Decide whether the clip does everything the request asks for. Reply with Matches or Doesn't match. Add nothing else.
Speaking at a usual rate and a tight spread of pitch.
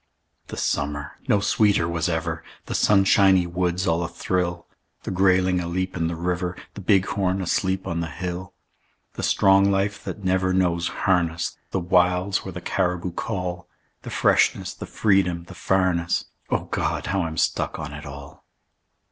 Matches